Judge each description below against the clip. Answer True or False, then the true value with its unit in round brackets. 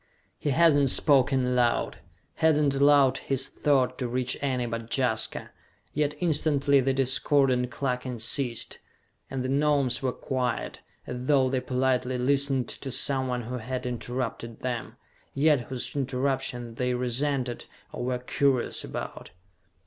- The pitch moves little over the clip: True (2.0 semitones)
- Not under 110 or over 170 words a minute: True (140 wpm)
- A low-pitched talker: True (130 Hz)